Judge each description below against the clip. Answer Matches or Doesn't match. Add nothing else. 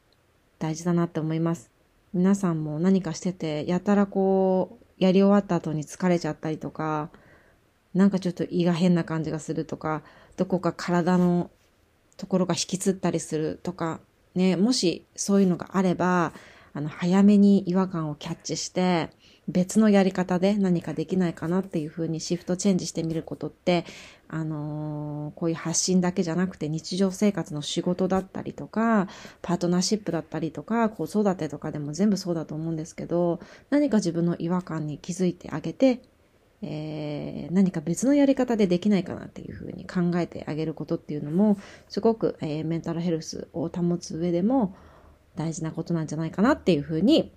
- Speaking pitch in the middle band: Matches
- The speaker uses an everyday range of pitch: Matches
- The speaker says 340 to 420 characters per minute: Matches